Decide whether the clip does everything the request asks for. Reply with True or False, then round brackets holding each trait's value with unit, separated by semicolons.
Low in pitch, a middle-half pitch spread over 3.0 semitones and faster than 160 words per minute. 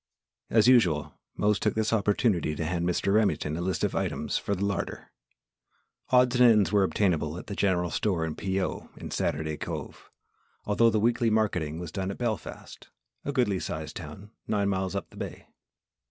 True (100 Hz; 3.8 semitones; 185 wpm)